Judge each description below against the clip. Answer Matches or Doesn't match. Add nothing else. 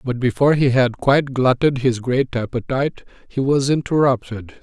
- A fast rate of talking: Doesn't match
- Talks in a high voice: Doesn't match